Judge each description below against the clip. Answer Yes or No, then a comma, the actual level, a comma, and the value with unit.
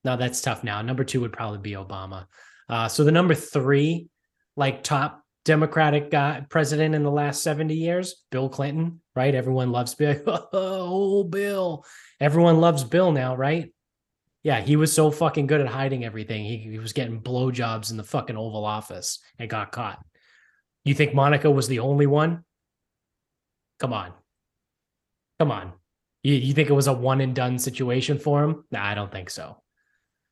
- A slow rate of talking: No, average, 175 wpm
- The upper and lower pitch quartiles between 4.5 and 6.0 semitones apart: No, average, 3.9 semitones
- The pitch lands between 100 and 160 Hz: Yes, medium, 140 Hz